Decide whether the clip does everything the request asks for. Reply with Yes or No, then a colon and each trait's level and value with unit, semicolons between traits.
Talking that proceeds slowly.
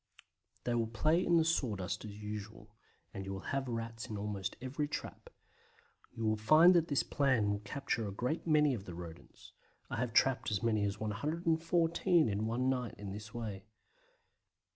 No: average, 180 wpm